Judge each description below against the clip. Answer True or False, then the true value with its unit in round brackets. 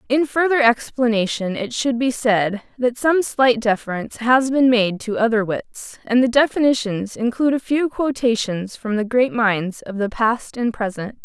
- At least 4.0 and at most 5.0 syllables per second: True (4.5 syllables/s)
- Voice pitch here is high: True (235 Hz)